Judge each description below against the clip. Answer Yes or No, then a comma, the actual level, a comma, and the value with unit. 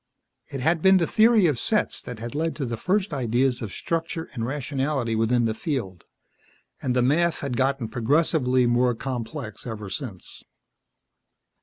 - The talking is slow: No, average, 160 wpm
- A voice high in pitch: No, low, 130 Hz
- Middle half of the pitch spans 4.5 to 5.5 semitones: Yes, average, 5.1 semitones